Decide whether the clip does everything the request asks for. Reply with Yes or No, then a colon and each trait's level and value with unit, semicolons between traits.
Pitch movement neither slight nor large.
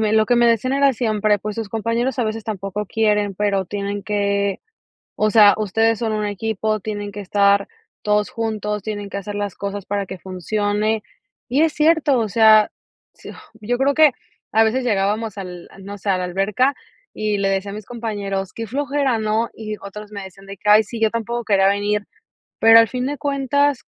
No: narrow, 2.1 semitones